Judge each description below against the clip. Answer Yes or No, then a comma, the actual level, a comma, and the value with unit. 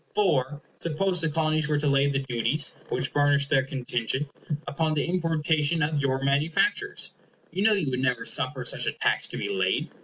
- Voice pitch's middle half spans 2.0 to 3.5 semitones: Yes, average, 3.0 semitones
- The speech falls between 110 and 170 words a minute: No, average, 185 wpm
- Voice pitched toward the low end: No, medium, 145 Hz